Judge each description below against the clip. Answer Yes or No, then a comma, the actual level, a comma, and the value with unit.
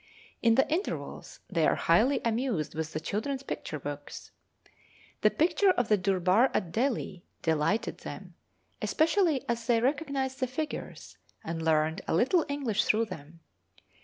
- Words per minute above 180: No, average, 145 wpm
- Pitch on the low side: No, high, 230 Hz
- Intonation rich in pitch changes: Yes, wide, 8.5 semitones